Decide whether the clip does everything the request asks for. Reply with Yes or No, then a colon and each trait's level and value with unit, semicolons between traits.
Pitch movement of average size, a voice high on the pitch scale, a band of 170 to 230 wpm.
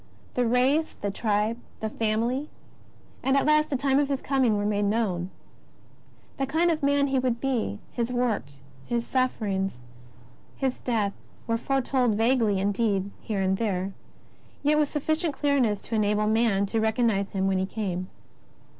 No: average, 4.7 semitones; high, 230 Hz; average, 160 wpm